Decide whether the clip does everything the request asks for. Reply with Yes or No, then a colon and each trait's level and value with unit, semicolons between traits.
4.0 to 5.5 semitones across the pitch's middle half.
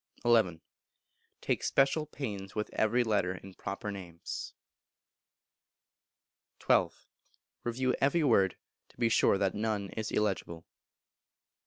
No: average, 3.6 semitones